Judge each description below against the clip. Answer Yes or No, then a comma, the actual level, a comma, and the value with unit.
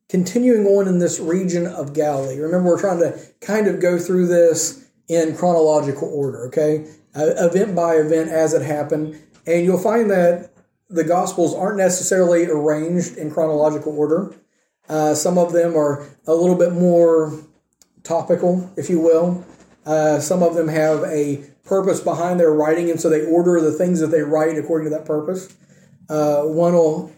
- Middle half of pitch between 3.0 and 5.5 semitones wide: No, narrow, 2.4 semitones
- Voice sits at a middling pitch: Yes, medium, 165 Hz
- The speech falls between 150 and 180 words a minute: Yes, average, 170 wpm